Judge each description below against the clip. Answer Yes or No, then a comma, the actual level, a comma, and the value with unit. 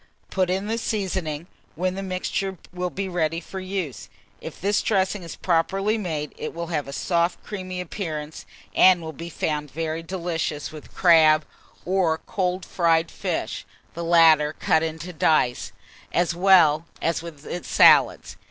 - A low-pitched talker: No, medium, 170 Hz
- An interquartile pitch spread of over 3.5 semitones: No, average, 2.7 semitones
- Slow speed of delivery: No, average, 150 wpm